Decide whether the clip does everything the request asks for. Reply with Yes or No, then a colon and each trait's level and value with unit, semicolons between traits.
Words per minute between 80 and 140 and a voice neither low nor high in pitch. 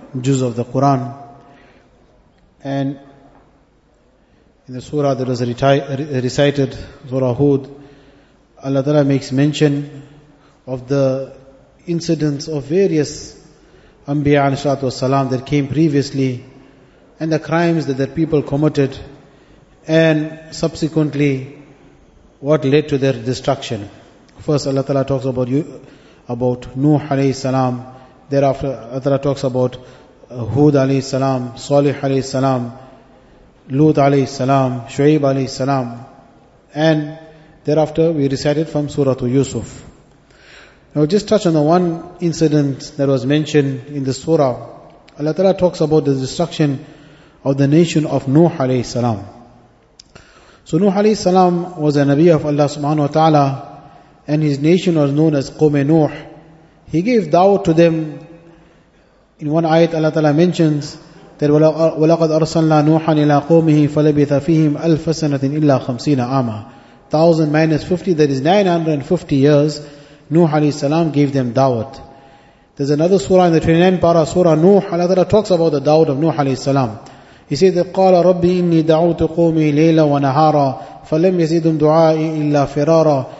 Yes: slow, 135 wpm; medium, 145 Hz